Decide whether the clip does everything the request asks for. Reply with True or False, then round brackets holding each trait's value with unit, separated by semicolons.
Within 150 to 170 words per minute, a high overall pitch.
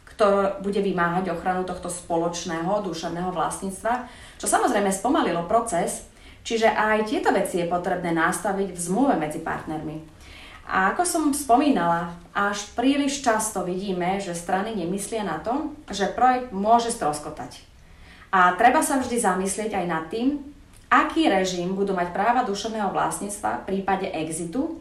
False (140 wpm; 195 Hz)